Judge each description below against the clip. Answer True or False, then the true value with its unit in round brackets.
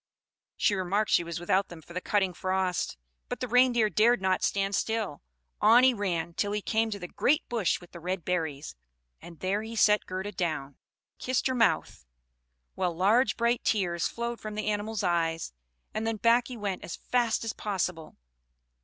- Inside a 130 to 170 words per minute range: False (185 wpm)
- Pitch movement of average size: True (4.2 semitones)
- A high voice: True (200 Hz)